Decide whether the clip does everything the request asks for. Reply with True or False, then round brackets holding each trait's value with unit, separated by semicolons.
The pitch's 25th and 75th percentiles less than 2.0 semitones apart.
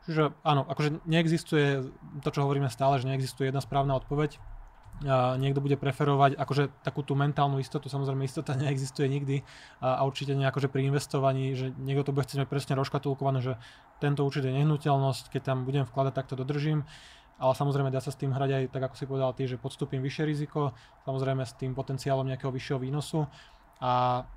True (1.2 semitones)